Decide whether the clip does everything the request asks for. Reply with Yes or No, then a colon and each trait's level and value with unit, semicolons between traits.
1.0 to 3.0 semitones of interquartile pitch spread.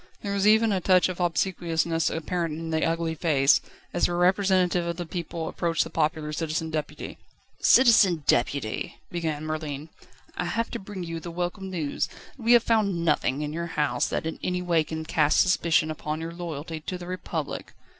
Yes: narrow, 2.5 semitones